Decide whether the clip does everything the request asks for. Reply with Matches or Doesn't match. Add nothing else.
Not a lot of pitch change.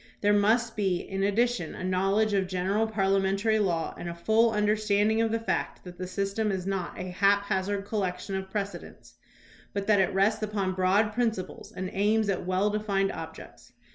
Matches